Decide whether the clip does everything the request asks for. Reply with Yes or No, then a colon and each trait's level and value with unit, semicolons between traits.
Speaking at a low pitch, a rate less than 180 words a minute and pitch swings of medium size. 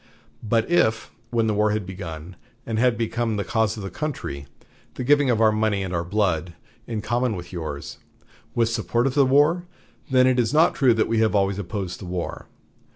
No: low, 110 Hz; fast, 205 wpm; average, 4.0 semitones